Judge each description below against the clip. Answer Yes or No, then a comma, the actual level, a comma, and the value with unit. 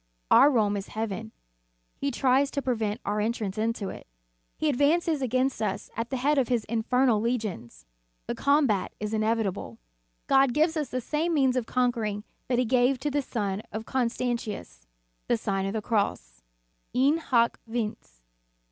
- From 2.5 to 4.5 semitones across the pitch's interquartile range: Yes, average, 4.1 semitones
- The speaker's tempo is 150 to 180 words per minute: Yes, average, 165 wpm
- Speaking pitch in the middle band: No, high, 235 Hz